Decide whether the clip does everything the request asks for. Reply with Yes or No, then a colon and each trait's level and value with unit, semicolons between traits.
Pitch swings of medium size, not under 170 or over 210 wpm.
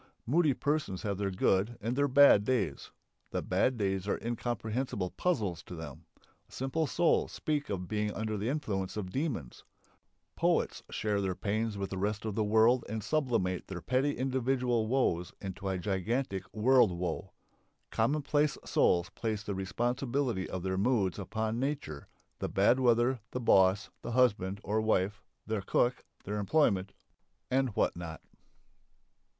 No: average, 4.9 semitones; average, 150 wpm